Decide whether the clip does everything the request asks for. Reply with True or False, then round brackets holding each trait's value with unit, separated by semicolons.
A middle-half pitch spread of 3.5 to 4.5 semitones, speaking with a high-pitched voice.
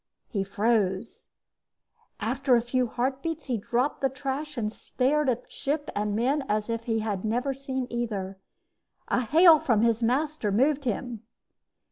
True (3.8 semitones; 245 Hz)